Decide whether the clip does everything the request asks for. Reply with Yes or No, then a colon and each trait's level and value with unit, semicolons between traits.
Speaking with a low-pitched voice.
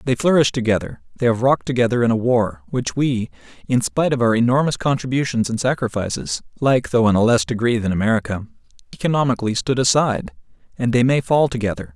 Yes: low, 125 Hz